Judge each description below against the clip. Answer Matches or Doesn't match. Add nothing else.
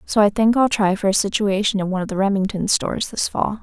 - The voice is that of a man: Doesn't match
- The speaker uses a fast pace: Matches